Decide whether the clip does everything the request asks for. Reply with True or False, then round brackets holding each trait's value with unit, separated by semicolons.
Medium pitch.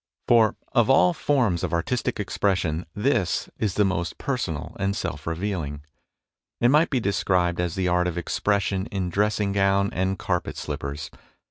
False (95 Hz)